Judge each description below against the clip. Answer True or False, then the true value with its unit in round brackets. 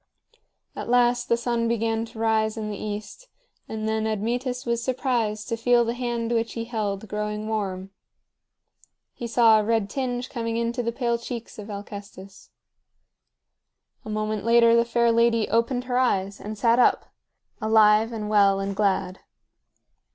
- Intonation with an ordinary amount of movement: False (1.9 semitones)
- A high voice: True (225 Hz)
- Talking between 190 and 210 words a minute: False (160 wpm)